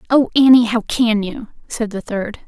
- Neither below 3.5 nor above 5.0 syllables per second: Yes, 4.5 syllables/s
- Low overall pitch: No, high, 225 Hz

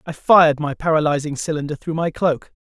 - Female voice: No, male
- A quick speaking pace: No, average, 180 wpm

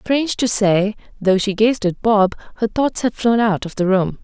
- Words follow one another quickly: Yes, fast, 225 wpm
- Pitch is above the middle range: Yes, high, 210 Hz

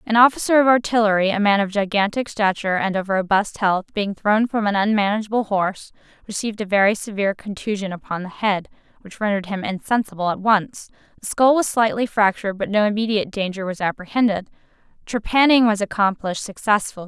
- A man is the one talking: No, female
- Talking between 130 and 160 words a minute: No, average, 170 wpm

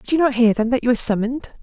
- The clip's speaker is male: No, female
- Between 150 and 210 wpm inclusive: No, fast, 335 wpm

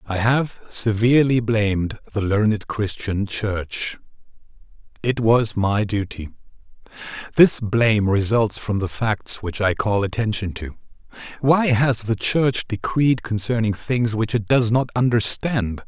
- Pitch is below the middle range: Yes, low, 110 Hz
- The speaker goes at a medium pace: No, slow, 130 wpm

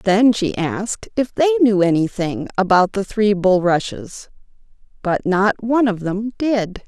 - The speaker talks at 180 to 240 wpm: No, average, 150 wpm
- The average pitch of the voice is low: No, high, 205 Hz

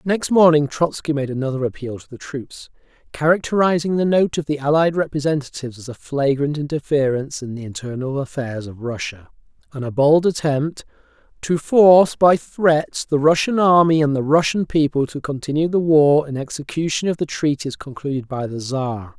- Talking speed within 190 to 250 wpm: No, average, 170 wpm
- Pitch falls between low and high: Yes, medium, 145 Hz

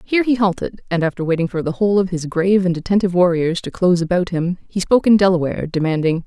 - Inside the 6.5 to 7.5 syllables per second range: Yes, 6.9 syllables/s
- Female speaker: Yes, female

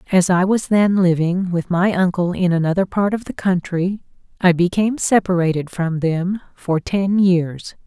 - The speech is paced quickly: No, average, 170 wpm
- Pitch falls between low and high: Yes, medium, 180 Hz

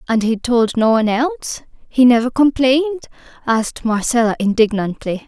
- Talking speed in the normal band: No, slow, 125 wpm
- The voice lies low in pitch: No, high, 240 Hz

